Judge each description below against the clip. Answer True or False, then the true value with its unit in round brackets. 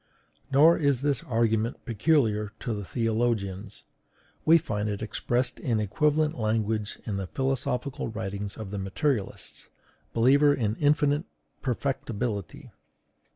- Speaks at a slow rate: True (115 wpm)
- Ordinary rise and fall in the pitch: True (4.9 semitones)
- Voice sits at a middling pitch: False (115 Hz)